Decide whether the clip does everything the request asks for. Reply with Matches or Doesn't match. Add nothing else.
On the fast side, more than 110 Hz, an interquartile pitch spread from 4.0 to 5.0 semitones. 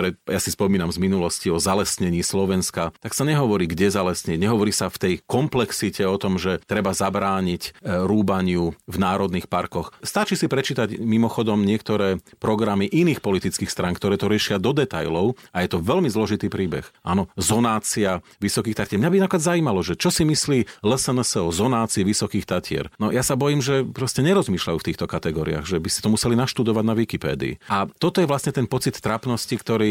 Doesn't match